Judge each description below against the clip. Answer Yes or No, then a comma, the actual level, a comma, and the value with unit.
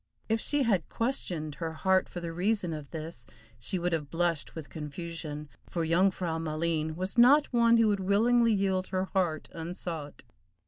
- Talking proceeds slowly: No, average, 175 wpm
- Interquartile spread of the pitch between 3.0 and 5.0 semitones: Yes, average, 3.8 semitones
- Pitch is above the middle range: No, medium, 175 Hz